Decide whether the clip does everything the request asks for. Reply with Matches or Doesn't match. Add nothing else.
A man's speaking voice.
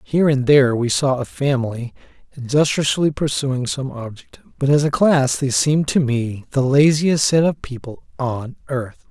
Matches